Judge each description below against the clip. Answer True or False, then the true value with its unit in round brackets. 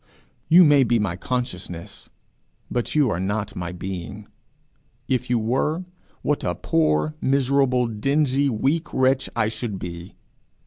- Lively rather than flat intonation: True (6.1 semitones)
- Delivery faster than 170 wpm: False (135 wpm)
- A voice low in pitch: True (120 Hz)